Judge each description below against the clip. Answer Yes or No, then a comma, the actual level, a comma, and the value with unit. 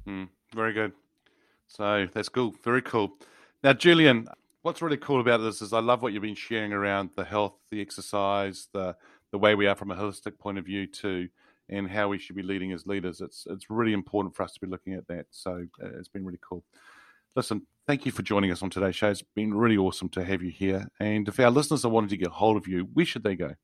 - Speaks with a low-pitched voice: Yes, low, 100 Hz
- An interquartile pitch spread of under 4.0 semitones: Yes, narrow, 2.6 semitones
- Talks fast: Yes, fast, 245 wpm